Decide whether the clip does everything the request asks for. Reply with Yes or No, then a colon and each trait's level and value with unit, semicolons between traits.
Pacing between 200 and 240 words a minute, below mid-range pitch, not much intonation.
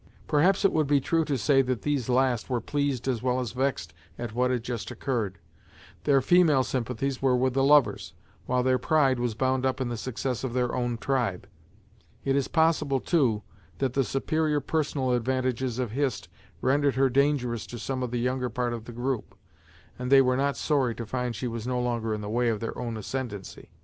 Yes: fast, 205 wpm; low, 130 Hz; narrow, 2.1 semitones